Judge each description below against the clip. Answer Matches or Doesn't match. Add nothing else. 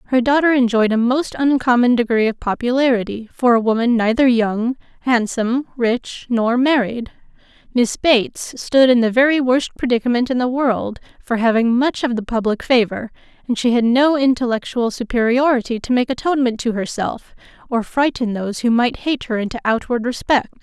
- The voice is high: Matches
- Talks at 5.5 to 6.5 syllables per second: Doesn't match